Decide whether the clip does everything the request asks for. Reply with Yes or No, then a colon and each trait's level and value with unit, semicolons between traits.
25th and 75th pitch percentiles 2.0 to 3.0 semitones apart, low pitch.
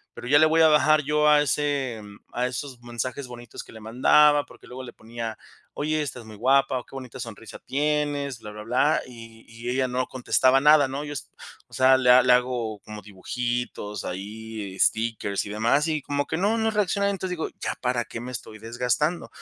No: average, 4.2 semitones; low, 125 Hz